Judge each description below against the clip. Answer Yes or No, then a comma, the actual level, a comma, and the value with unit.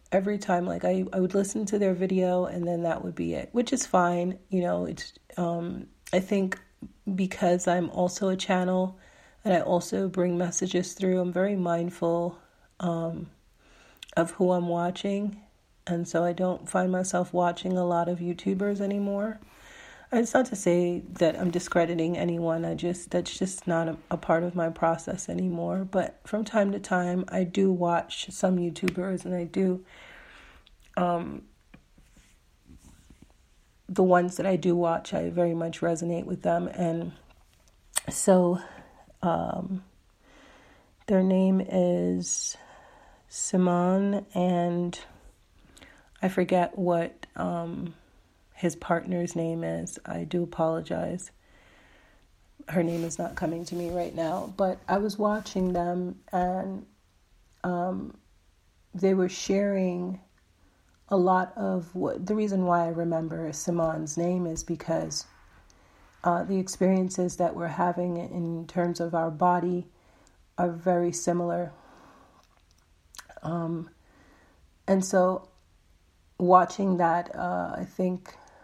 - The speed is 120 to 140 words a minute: Yes, slow, 135 wpm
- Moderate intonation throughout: No, narrow, 1.8 semitones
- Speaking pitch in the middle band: Yes, medium, 175 Hz